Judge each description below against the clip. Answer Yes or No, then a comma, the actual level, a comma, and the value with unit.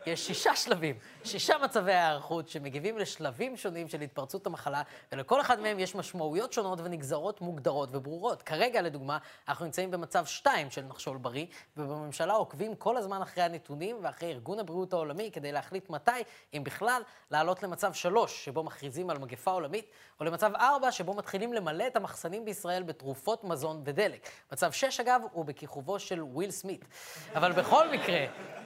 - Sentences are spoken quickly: Yes, fast, 160 wpm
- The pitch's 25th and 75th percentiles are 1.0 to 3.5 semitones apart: No, average, 5.3 semitones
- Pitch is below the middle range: No, medium, 175 Hz